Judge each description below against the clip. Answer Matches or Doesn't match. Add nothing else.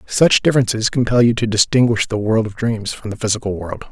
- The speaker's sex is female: Doesn't match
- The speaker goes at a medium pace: Doesn't match